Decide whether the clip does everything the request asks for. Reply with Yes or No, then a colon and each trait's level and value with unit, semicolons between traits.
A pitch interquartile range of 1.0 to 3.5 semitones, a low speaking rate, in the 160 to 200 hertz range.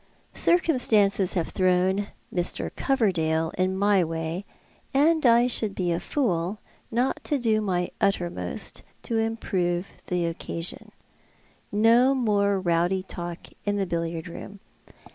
No: average, 4.3 semitones; slow, 125 wpm; high, 190 Hz